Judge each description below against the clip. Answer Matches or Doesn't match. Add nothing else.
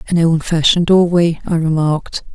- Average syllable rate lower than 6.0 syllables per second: Matches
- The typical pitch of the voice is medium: Matches